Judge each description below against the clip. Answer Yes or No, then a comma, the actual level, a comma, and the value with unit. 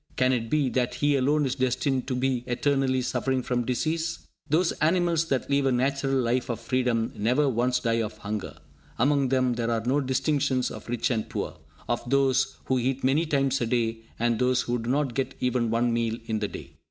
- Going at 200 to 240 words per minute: Yes, fast, 205 wpm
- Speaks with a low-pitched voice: Yes, low, 130 Hz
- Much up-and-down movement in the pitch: No, narrow, 2.4 semitones